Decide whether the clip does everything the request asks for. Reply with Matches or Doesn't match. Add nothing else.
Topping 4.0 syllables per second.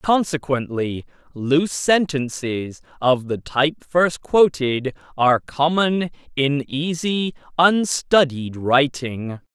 Doesn't match